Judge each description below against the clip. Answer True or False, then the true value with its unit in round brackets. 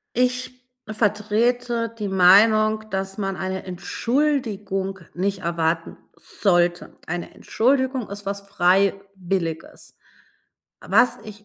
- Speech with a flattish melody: False (3.2 semitones)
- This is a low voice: False (200 Hz)